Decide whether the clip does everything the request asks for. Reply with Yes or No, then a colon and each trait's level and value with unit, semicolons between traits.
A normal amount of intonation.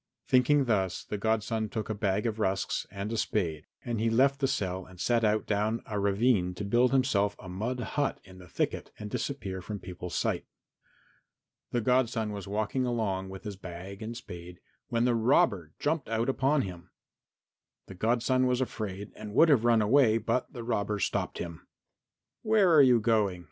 Yes: average, 4.0 semitones